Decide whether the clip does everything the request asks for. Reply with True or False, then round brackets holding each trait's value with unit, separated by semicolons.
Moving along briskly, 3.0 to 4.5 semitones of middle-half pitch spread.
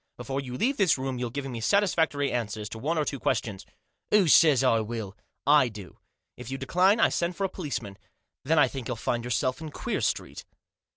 False (215 wpm; 5.3 semitones)